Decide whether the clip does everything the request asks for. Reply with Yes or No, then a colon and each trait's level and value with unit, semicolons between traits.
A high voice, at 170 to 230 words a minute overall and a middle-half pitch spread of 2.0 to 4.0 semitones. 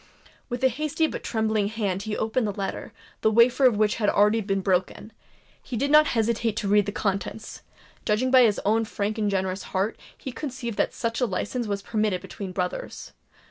Yes: high, 220 Hz; average, 185 wpm; average, 2.7 semitones